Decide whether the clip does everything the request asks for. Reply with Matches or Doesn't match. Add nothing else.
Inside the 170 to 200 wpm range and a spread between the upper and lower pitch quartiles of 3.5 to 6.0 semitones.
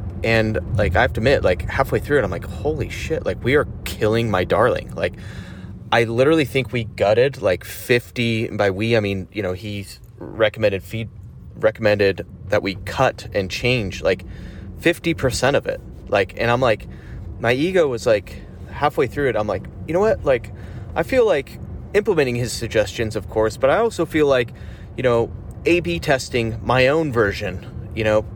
Matches